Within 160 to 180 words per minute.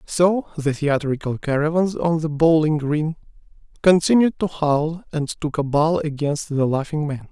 No: average, 150 wpm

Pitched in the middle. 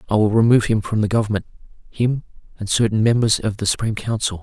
No: low, 110 Hz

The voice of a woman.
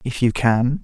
No: male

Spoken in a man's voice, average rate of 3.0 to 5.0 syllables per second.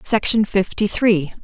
No: female; 4.0 syllables/s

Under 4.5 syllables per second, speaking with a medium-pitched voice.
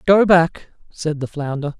Yes: 4.0 syllables/s; medium, 160 Hz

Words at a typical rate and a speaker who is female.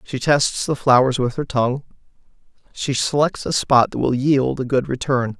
No: average, 190 wpm; male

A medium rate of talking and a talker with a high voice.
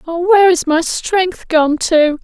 Yes: average, 190 wpm; very high, 340 Hz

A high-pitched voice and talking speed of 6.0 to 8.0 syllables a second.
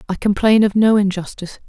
Yes: high, 205 Hz; 6.2 syllables/s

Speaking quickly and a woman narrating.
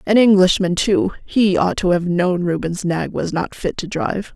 No: average, 195 wpm; female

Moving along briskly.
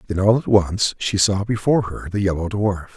Yes: fast, 225 wpm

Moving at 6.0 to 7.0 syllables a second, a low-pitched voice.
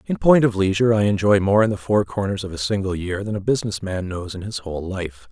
Yes: 6.2 syllables/s; low, 100 Hz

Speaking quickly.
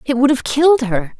Yes: fast, 250 wpm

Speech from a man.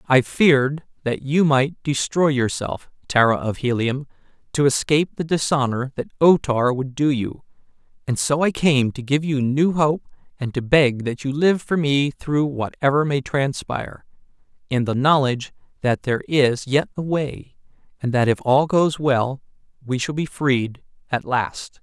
Yes: male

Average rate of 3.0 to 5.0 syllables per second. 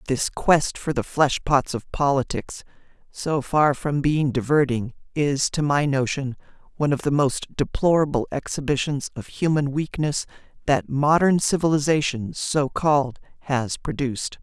Yes: 4.5 syllables/s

